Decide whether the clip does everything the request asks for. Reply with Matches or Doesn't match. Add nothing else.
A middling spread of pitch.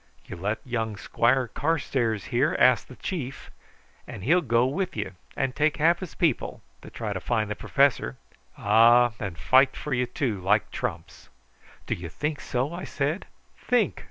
Matches